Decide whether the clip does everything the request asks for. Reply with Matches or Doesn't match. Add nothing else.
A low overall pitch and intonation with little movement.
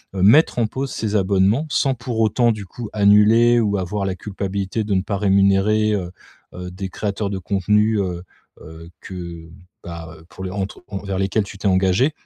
Matches